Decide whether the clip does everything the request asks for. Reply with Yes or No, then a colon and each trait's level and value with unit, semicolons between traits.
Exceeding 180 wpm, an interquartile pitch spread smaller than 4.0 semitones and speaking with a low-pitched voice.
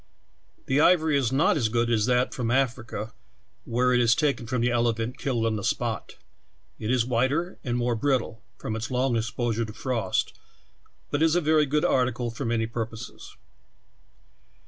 No: average, 170 wpm; average, 2.7 semitones; low, 120 Hz